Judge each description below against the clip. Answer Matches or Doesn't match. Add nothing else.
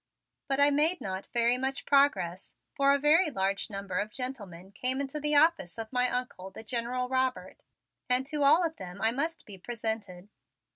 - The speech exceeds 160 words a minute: Matches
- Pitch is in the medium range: Doesn't match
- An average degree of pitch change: Doesn't match